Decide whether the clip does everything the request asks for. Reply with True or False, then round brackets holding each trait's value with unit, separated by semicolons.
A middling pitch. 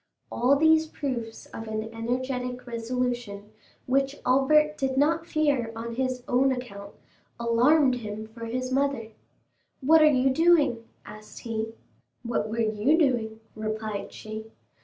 False (250 Hz)